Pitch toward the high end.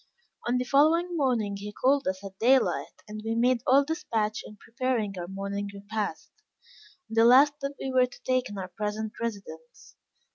Yes: high, 225 Hz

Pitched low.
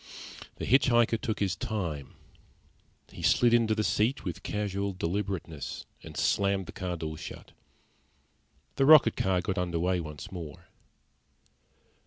Yes: very low, 95 Hz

